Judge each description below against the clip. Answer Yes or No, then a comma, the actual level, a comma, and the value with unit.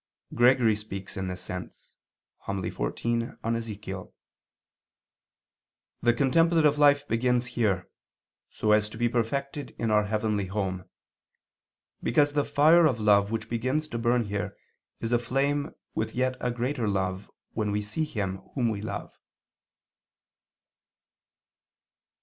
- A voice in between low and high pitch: No, low, 115 Hz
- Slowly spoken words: Yes, slow, 125 wpm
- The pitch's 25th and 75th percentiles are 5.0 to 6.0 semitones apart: No, average, 3.8 semitones